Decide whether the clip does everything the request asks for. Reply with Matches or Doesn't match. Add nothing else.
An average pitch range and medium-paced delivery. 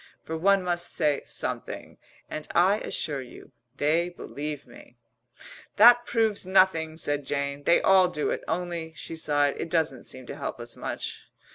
Matches